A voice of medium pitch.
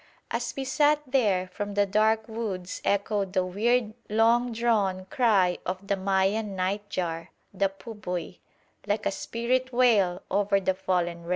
No: high, 200 Hz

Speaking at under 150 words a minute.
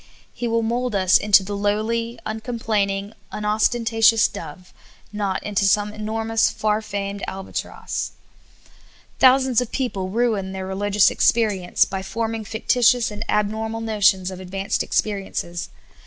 Yes: slow, 135 wpm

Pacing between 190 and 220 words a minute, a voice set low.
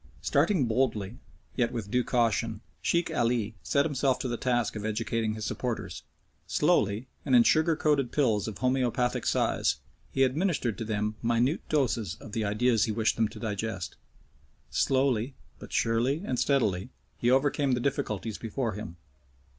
No: average, 155 wpm; low, 120 Hz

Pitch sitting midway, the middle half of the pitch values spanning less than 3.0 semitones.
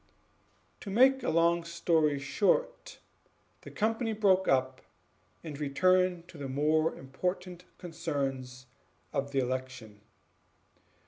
No: medium, 160 Hz; wide, 5.4 semitones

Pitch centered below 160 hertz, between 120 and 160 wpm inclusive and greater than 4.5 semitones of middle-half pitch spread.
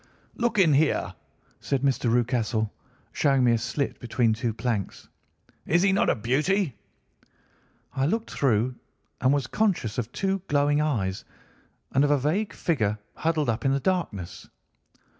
Yes: low, 135 Hz; average, 150 wpm; average, 5.2 semitones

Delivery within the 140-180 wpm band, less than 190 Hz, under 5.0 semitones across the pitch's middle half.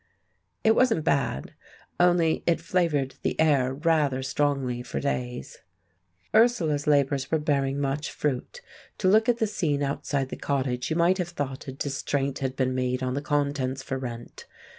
Yes: average, 160 wpm; medium, 140 Hz; average, 3.7 semitones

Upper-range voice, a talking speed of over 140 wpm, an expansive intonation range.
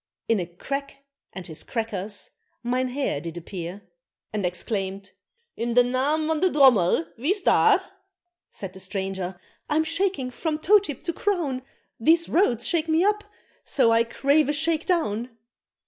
Yes: very high, 255 Hz; average, 150 wpm; wide, 8.1 semitones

